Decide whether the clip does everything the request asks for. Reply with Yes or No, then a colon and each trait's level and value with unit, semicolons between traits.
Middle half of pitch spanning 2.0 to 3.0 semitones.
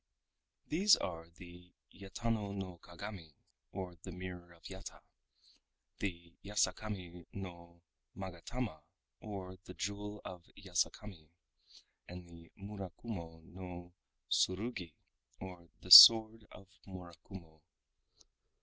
Yes: average, 2.7 semitones